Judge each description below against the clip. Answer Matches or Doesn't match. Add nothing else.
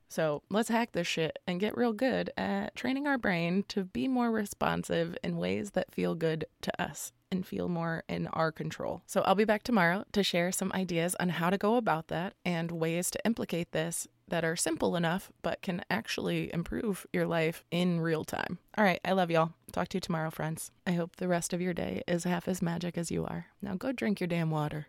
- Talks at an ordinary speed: Doesn't match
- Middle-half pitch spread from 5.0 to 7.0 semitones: Doesn't match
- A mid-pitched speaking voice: Matches